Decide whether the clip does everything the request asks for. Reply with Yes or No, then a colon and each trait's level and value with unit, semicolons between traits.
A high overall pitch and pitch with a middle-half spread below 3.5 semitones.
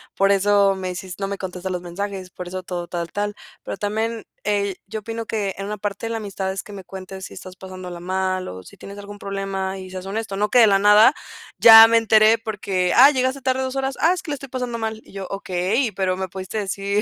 Yes: high, 200 Hz; average, 2.8 semitones